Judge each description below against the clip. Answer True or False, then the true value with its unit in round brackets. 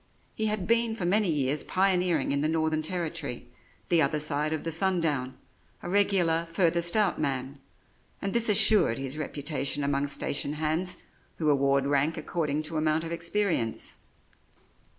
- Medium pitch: True (160 Hz)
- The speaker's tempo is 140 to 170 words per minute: True (155 wpm)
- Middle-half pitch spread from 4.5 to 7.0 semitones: False (4.0 semitones)